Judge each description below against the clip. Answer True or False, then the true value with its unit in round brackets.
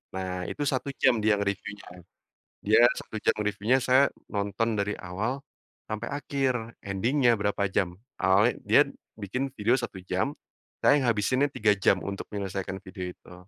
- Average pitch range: True (4.2 semitones)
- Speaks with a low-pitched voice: True (105 Hz)